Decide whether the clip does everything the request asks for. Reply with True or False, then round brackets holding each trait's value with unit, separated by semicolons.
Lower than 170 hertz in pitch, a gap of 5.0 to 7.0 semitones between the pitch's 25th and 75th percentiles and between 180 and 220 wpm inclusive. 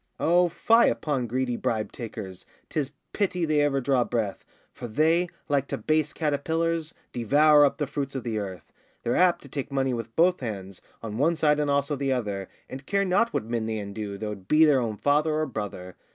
True (140 Hz; 5.6 semitones; 205 wpm)